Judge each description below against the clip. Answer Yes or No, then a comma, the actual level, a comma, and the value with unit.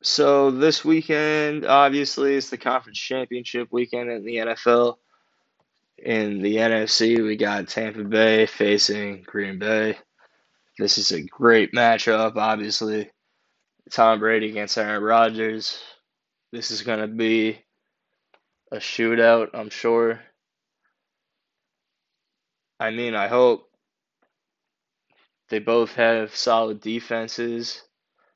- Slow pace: Yes, slow, 110 wpm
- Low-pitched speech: Yes, low, 115 Hz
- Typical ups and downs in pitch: No, narrow, 1.6 semitones